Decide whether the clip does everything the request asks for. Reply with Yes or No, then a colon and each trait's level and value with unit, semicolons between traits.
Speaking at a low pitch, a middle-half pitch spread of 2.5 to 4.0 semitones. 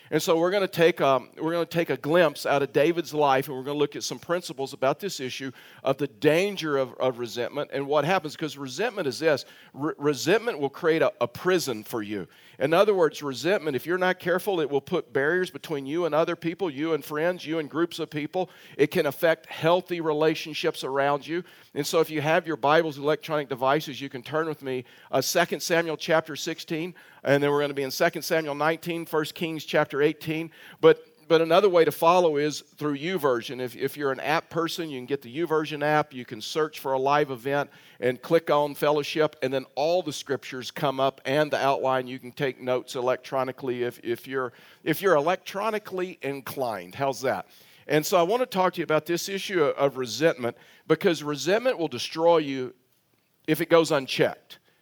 No: medium, 150 Hz; average, 3.6 semitones